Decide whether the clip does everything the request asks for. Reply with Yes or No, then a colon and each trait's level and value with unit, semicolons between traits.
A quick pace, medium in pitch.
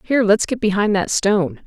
No: fast, 215 wpm; high, 210 Hz